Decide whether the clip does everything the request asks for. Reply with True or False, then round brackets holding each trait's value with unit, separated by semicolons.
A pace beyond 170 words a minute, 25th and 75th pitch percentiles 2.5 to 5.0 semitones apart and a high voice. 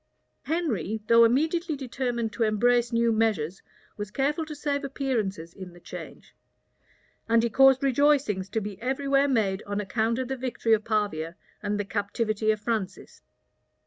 False (160 wpm; 4.5 semitones; 230 Hz)